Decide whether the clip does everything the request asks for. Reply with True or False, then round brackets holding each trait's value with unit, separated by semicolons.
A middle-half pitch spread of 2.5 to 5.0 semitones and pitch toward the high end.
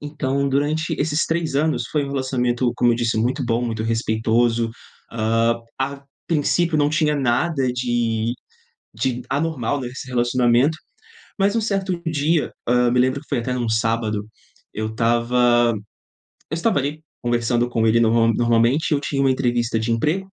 False (3.8 semitones; 125 Hz)